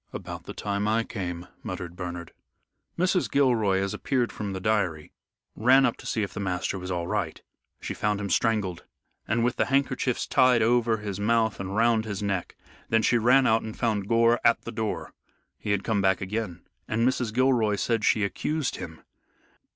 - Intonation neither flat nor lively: Yes, average, 3.3 semitones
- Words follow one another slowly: No, average, 190 wpm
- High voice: No, low, 110 Hz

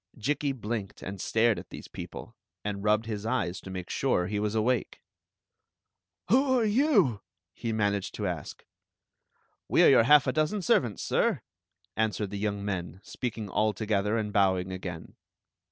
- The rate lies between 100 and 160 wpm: No, average, 170 wpm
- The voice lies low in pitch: Yes, low, 105 Hz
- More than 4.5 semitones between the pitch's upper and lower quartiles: No, average, 3.6 semitones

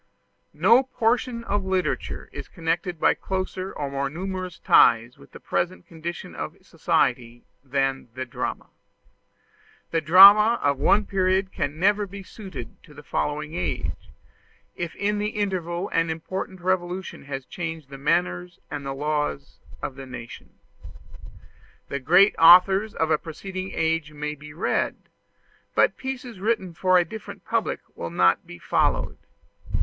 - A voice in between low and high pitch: Yes, medium, 170 Hz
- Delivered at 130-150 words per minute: Yes, average, 145 wpm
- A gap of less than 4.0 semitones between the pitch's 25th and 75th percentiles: No, average, 5.0 semitones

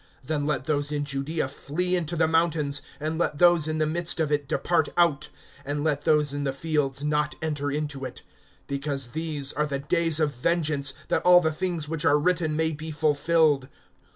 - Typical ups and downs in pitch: No, narrow, 2.1 semitones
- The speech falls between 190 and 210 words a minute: Yes, average, 195 wpm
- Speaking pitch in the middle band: Yes, medium, 150 Hz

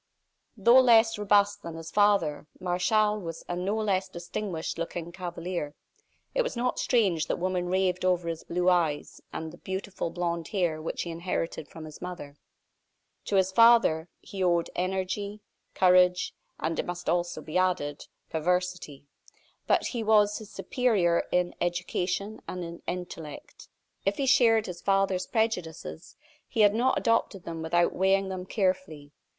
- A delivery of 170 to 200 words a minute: No, average, 155 wpm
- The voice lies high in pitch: No, medium, 180 Hz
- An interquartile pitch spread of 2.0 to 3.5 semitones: Yes, average, 3.2 semitones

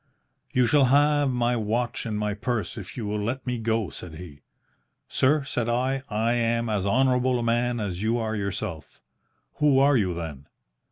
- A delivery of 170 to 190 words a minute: Yes, average, 180 wpm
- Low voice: Yes, low, 115 Hz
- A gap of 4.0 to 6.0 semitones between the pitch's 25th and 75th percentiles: No, average, 3.4 semitones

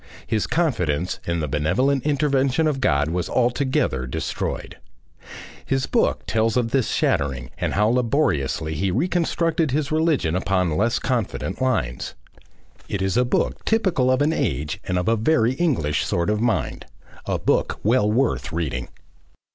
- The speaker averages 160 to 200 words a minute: No, average, 150 wpm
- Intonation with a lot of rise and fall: Yes, wide, 8.1 semitones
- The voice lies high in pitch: No, low, 115 Hz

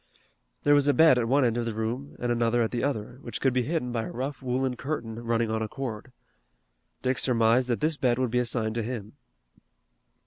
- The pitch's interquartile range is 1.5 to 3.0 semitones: Yes, narrow, 2.5 semitones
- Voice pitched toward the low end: Yes, low, 120 Hz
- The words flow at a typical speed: No, fast, 220 wpm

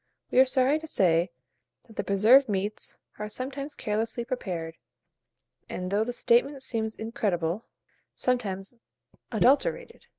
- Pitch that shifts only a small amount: No, average, 4.8 semitones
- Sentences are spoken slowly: Yes, slow, 125 wpm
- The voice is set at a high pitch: Yes, high, 225 Hz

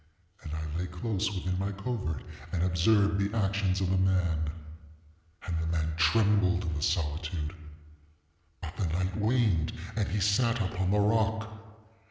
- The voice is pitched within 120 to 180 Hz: No, very low, 95 Hz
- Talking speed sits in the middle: Yes, average, 150 wpm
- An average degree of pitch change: Yes, average, 3.9 semitones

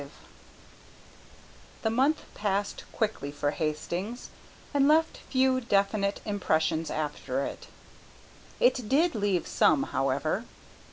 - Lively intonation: Yes, wide, 8.5 semitones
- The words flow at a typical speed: No, slow, 105 wpm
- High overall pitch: Yes, high, 200 Hz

